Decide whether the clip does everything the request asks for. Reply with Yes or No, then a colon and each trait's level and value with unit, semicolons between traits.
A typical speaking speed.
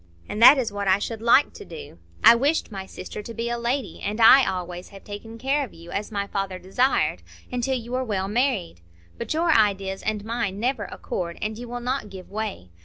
No: fast, 220 wpm